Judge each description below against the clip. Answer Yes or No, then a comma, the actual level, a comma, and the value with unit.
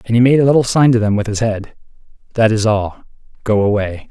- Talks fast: Yes, fast, 235 wpm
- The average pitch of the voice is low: Yes, low, 110 Hz